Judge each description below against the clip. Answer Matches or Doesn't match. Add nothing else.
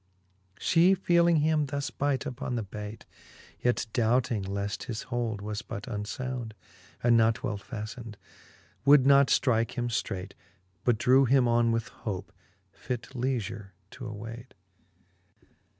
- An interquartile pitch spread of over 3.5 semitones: Doesn't match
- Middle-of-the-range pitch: Doesn't match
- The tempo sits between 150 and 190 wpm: Doesn't match